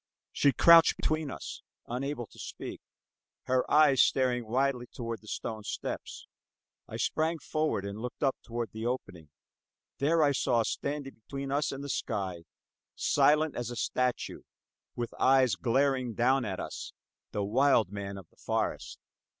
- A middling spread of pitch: Yes, average, 3.8 semitones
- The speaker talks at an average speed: Yes, average, 150 wpm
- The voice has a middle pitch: No, low, 125 Hz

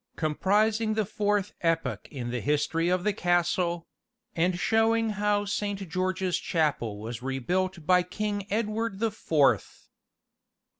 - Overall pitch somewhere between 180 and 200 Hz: Yes, medium, 185 Hz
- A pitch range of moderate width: Yes, average, 4.6 semitones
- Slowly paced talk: Yes, slow, 130 wpm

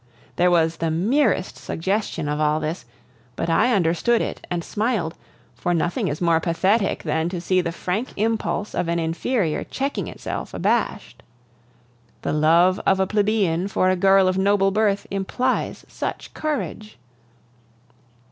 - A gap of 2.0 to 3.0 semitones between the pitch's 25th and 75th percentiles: No, average, 4.1 semitones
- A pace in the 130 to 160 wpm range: Yes, average, 145 wpm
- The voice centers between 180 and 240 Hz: Yes, medium, 185 Hz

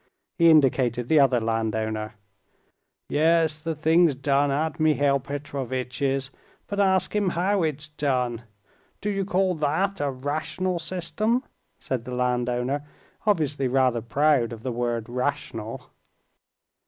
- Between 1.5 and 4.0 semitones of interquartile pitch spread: No, average, 4.5 semitones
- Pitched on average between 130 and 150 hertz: Yes, medium, 140 Hz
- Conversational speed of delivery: No, slow, 125 wpm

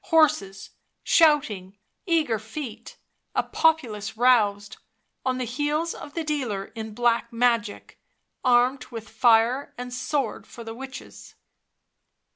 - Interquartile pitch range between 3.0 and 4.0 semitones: No, average, 4.4 semitones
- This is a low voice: No, high, 245 Hz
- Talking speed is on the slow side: Yes, slow, 115 wpm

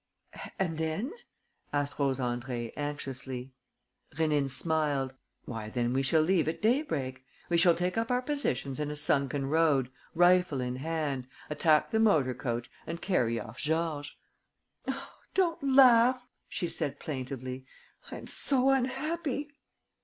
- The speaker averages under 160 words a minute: Yes, average, 140 wpm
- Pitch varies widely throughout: Yes, wide, 5.8 semitones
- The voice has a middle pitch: Yes, medium, 150 Hz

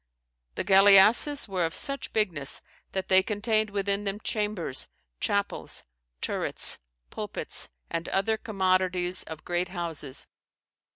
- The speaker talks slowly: Yes, slow, 115 wpm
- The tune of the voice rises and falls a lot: No, average, 2.8 semitones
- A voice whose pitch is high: Yes, high, 195 Hz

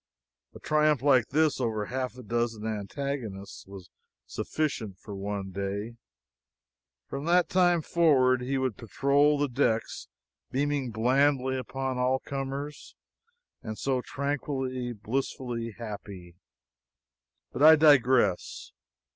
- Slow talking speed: Yes, slow, 115 wpm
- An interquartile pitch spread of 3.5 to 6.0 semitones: Yes, average, 4.2 semitones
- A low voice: Yes, low, 130 Hz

